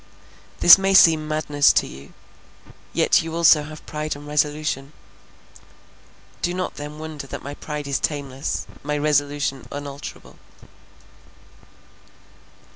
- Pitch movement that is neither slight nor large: No, narrow, 1.3 semitones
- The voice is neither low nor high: Yes, medium, 150 Hz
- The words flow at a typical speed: No, slow, 120 wpm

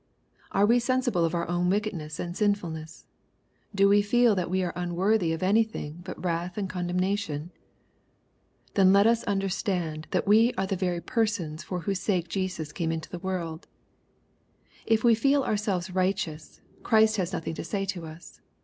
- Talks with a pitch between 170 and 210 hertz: Yes, medium, 185 Hz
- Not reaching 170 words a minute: No, average, 175 wpm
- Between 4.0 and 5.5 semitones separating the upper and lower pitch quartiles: No, average, 3.3 semitones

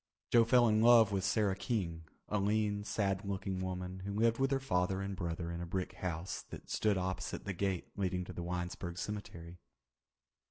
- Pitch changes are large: No, narrow, 2.6 semitones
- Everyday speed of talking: Yes, average, 190 wpm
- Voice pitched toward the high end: No, very low, 95 Hz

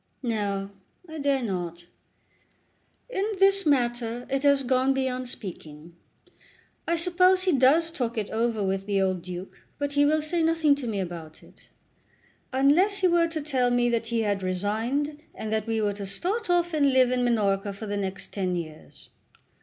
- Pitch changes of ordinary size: No, wide, 6.8 semitones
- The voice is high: Yes, high, 245 Hz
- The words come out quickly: No, average, 175 wpm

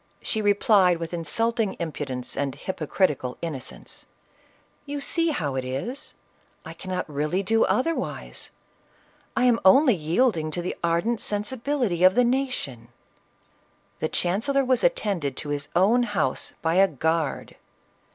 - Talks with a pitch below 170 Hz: No, high, 190 Hz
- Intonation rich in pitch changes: Yes, wide, 7.6 semitones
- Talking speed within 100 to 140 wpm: Yes, slow, 135 wpm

